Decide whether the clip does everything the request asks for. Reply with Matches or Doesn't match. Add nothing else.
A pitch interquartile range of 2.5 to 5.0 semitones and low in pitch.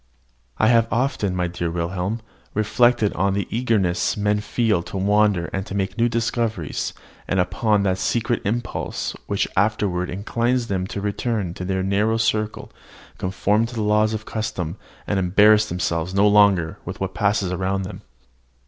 Matches